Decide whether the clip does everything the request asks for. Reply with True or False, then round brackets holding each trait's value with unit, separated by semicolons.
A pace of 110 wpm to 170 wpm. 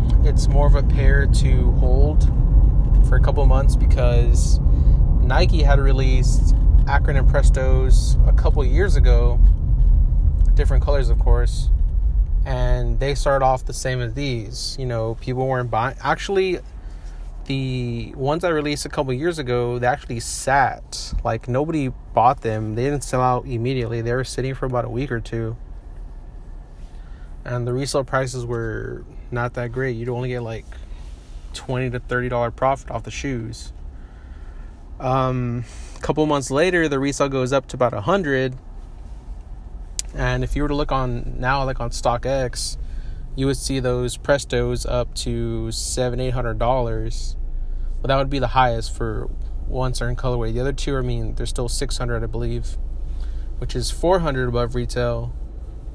True (160 wpm)